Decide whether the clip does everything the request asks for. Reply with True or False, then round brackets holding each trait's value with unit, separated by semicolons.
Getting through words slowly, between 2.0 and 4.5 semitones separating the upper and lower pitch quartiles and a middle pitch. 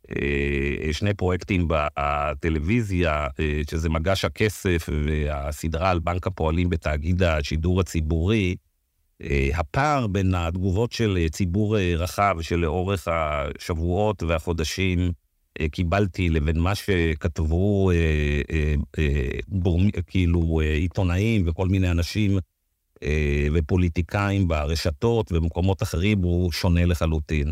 False (85 wpm; 3.3 semitones; 85 Hz)